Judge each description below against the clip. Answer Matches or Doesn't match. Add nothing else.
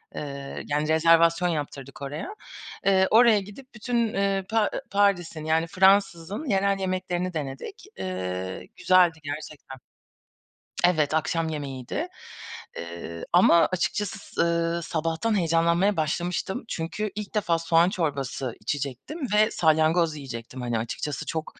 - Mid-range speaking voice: Matches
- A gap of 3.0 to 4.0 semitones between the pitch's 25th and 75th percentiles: Doesn't match